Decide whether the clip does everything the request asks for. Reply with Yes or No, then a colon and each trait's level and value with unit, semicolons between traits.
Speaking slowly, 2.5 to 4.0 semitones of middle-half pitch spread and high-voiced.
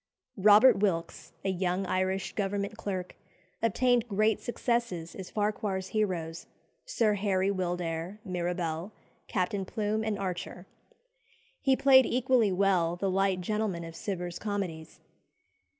Yes: slow, 120 wpm; average, 3.1 semitones; high, 195 Hz